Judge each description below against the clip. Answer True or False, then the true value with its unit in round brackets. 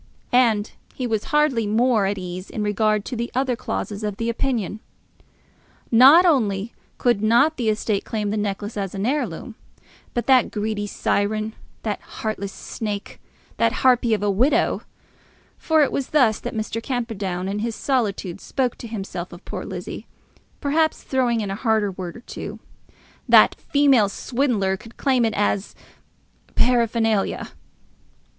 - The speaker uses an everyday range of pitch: True (3.5 semitones)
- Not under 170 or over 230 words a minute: False (150 wpm)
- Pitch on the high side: True (220 Hz)